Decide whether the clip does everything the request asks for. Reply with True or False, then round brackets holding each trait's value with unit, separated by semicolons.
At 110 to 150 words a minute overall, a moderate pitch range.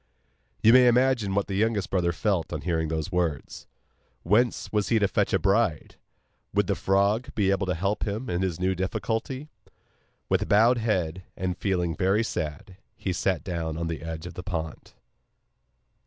False (175 wpm; 3.7 semitones)